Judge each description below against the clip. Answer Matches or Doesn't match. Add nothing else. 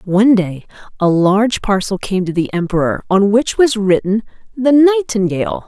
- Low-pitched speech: Doesn't match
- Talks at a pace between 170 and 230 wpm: Doesn't match